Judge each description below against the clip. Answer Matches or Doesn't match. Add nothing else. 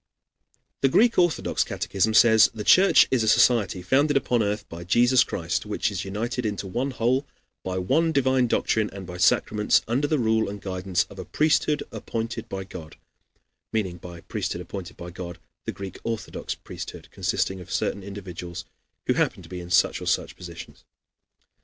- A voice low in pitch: Matches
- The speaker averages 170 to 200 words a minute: Matches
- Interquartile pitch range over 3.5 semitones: Matches